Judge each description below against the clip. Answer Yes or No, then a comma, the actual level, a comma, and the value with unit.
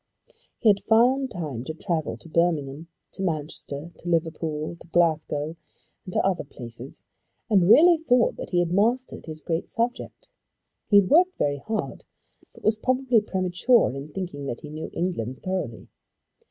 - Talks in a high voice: No, medium, 175 Hz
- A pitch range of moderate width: No, wide, 6.1 semitones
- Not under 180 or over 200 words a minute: No, average, 160 wpm